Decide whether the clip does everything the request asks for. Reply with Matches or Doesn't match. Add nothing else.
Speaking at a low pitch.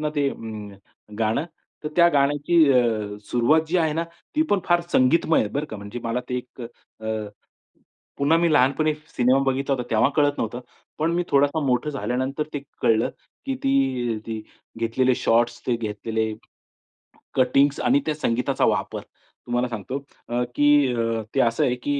Matches